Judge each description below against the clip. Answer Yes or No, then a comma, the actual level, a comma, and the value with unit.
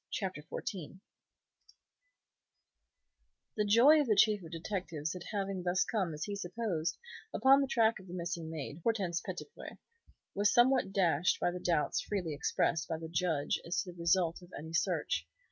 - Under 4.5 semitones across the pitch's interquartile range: Yes, average, 4.0 semitones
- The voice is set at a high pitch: No, medium, 180 Hz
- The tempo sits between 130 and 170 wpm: Yes, average, 165 wpm